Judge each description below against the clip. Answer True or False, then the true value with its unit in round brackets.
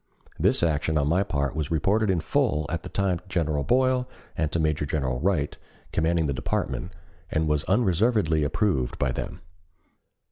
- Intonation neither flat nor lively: True (4.6 semitones)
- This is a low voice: True (80 Hz)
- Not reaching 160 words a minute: False (170 wpm)